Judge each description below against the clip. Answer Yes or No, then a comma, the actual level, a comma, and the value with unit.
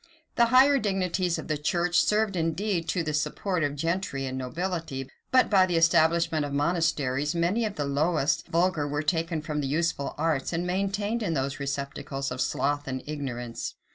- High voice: No, medium, 165 Hz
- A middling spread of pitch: Yes, average, 4.1 semitones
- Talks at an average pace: Yes, average, 175 wpm